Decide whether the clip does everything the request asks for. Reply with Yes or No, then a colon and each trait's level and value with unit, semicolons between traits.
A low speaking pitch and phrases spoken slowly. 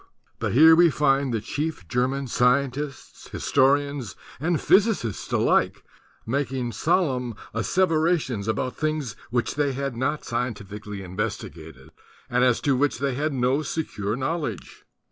Yes: low, 130 Hz; slow, 125 wpm